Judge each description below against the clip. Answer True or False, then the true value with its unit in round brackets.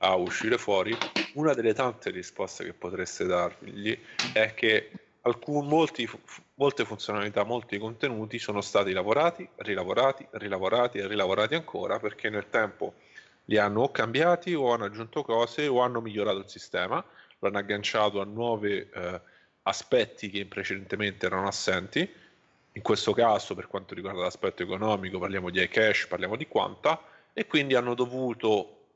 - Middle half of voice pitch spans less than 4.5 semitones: True (3.5 semitones)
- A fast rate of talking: False (150 wpm)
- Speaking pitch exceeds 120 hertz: False (110 Hz)